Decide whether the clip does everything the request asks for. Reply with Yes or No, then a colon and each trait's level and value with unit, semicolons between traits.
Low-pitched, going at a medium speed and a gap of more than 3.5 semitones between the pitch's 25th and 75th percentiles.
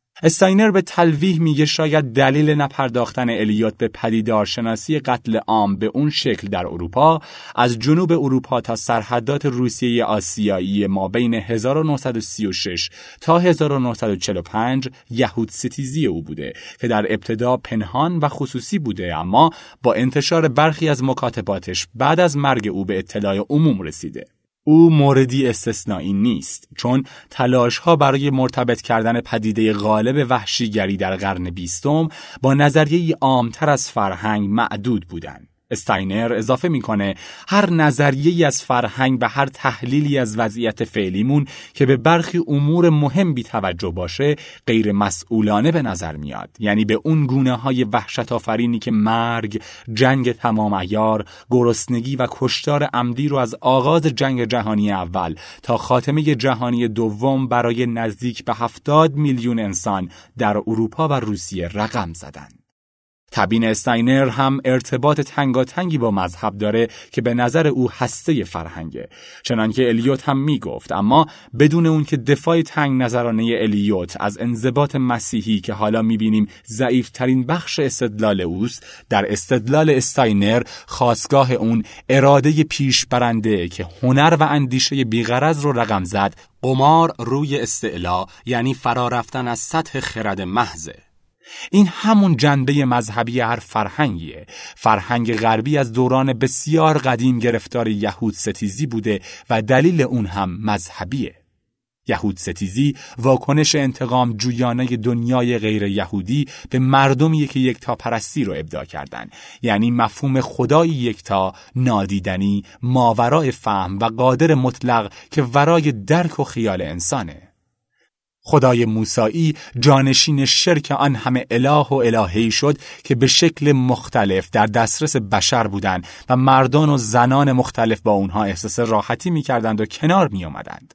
Yes: low, 120 Hz; average, 135 wpm; average, 4.4 semitones